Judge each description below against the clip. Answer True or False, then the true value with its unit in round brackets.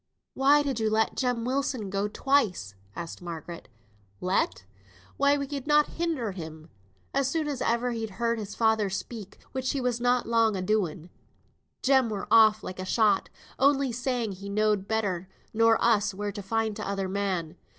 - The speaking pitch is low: False (220 Hz)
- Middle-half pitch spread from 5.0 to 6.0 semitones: False (4.3 semitones)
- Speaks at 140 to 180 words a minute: True (170 wpm)